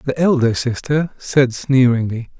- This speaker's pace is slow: Yes, slow, 125 wpm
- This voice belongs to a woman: No, male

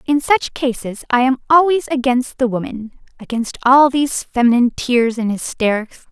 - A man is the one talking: No, female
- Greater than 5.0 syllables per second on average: No, 4.9 syllables/s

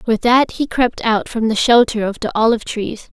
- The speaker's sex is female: Yes, female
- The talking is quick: Yes, fast, 225 wpm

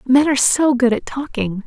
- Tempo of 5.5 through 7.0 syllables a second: No, 5.1 syllables/s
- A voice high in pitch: Yes, very high, 260 Hz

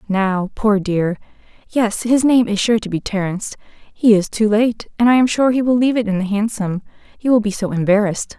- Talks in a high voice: Yes, high, 215 Hz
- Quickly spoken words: Yes, fast, 220 wpm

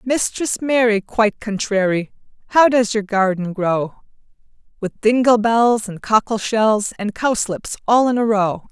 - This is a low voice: No, high, 220 Hz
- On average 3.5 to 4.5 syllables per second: Yes, 4.1 syllables/s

